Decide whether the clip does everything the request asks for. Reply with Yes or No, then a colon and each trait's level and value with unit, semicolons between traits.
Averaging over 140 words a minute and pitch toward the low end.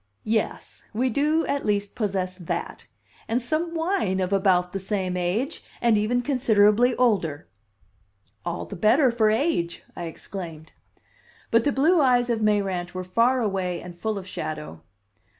No: average, 150 wpm; high, 210 Hz